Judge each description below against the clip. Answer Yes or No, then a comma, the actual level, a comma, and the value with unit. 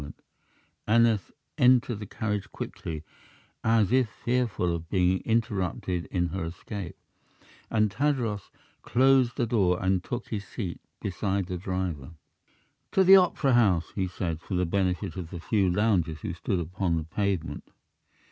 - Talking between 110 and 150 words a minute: Yes, average, 145 wpm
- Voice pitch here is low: Yes, very low, 95 Hz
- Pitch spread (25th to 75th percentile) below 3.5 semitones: No, average, 4.3 semitones